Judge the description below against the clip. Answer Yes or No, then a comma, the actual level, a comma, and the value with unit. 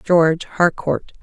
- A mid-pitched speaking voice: Yes, medium, 165 Hz